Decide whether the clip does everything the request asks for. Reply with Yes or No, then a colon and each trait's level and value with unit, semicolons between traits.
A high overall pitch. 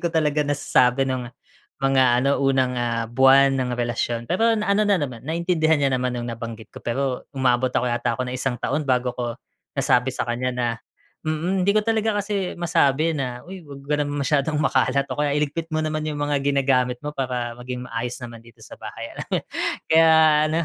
No: low, 135 Hz